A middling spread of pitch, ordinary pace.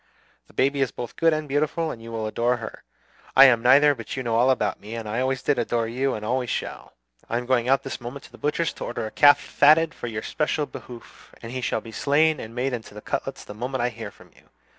No: average, 3.4 semitones; fast, 255 wpm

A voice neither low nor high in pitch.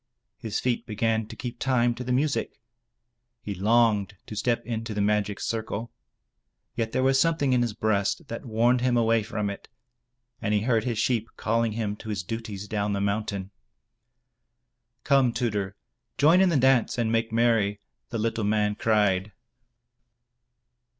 No: low, 115 Hz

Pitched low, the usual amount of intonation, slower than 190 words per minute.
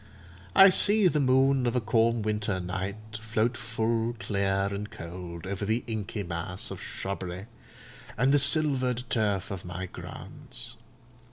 Yes: low, 110 Hz; average, 4.2 semitones; average, 145 wpm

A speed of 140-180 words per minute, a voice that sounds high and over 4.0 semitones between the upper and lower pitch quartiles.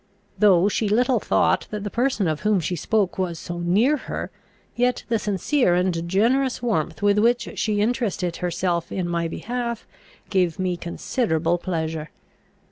Yes: average, 155 wpm; high, 195 Hz; average, 5.1 semitones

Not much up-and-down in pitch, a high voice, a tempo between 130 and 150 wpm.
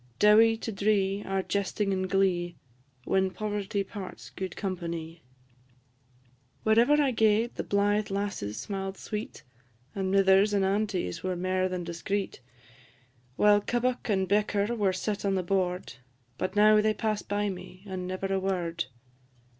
Yes: narrow, 2.0 semitones; high, 195 Hz; average, 145 wpm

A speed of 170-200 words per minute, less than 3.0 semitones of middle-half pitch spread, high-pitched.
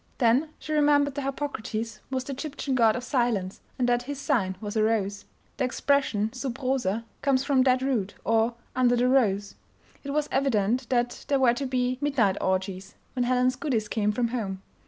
No: average, 185 wpm; average, 3.9 semitones; very high, 250 Hz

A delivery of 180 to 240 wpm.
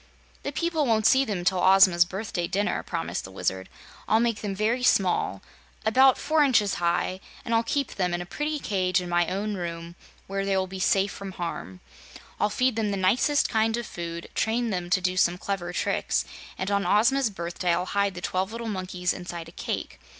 Yes: average, 200 wpm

